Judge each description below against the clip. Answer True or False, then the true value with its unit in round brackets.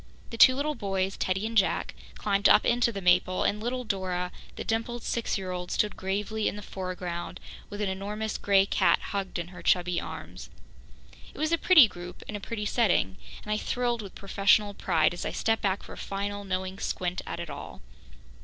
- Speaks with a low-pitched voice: False (200 Hz)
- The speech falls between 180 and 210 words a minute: True (200 wpm)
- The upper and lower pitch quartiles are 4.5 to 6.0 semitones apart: False (3.0 semitones)